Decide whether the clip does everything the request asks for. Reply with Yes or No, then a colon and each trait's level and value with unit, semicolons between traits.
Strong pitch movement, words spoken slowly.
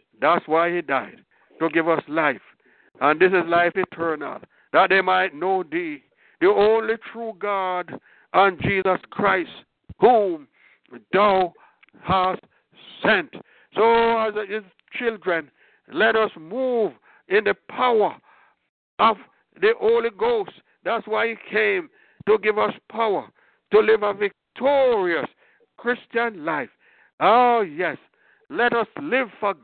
Yes: wide, 5.8 semitones; slow, 130 wpm